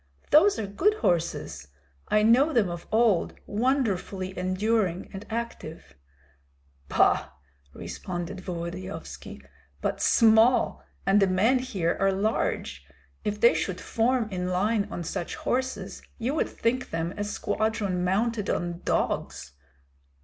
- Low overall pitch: No, high, 205 Hz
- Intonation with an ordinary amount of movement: Yes, average, 4.2 semitones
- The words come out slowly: Yes, slow, 125 wpm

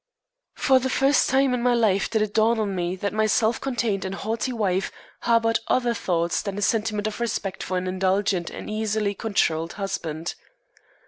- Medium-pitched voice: No, high, 215 Hz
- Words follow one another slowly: No, average, 185 wpm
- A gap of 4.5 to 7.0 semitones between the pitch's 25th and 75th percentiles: No, average, 3.4 semitones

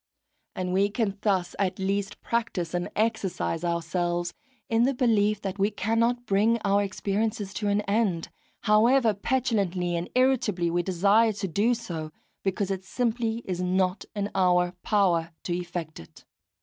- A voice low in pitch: No, high, 200 Hz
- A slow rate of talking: No, average, 150 wpm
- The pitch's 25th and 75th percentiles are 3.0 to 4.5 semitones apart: Yes, average, 3.8 semitones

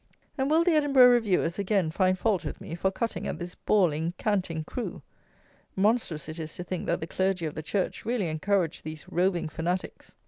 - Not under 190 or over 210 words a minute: Yes, average, 195 wpm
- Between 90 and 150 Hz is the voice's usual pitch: No, medium, 185 Hz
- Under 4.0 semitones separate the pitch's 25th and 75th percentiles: No, average, 4.6 semitones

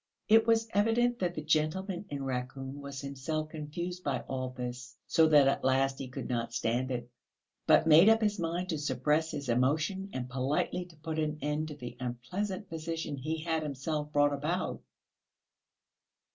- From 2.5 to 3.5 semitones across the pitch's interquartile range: No, average, 4.3 semitones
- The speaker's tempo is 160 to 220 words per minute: Yes, average, 175 wpm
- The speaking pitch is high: No, medium, 150 Hz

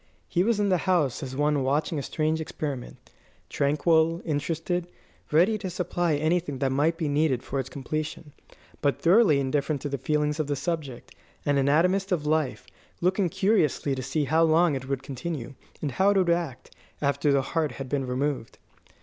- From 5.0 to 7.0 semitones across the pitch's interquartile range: No, average, 3.4 semitones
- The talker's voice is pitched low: No, medium, 150 Hz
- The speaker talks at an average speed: Yes, average, 180 wpm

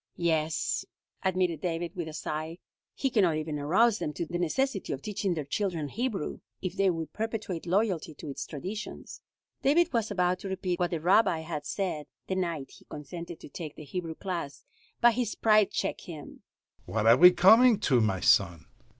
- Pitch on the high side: No, medium, 175 Hz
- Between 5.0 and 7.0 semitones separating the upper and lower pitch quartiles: No, average, 4.4 semitones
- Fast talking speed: No, average, 185 wpm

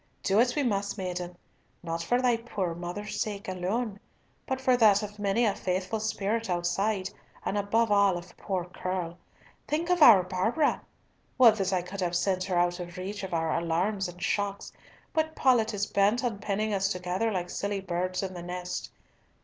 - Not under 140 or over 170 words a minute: No, average, 185 wpm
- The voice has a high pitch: Yes, high, 195 Hz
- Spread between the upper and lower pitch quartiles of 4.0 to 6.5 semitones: No, average, 3.3 semitones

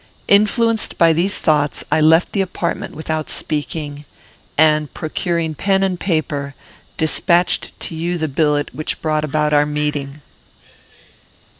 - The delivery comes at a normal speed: No, slow, 130 wpm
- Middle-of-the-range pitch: Yes, medium, 155 Hz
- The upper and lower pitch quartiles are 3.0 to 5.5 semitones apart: No, narrow, 2.6 semitones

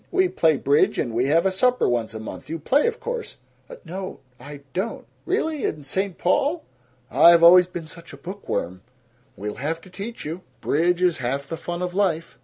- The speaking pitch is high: No, medium, 170 Hz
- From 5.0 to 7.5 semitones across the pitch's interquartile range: Yes, wide, 5.5 semitones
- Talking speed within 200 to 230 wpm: Yes, fast, 205 wpm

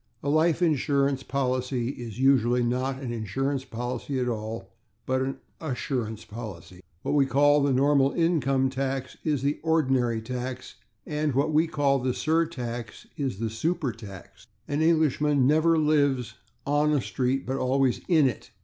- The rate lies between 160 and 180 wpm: No, average, 150 wpm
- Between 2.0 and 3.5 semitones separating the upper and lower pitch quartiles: Yes, average, 3.1 semitones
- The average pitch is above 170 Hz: No, low, 135 Hz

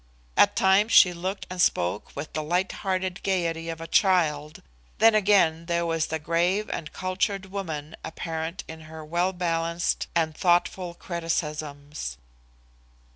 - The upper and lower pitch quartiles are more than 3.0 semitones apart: No, average, 2.7 semitones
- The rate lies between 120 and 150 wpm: Yes, average, 140 wpm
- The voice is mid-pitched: Yes, medium, 170 Hz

